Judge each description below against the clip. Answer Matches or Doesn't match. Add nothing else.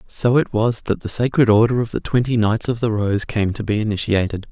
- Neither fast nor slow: Doesn't match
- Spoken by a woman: Doesn't match